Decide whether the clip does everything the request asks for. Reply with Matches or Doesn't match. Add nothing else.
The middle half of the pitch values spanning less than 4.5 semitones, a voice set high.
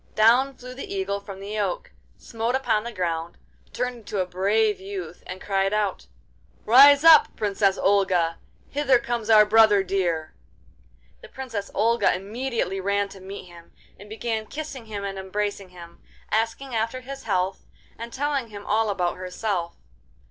Matches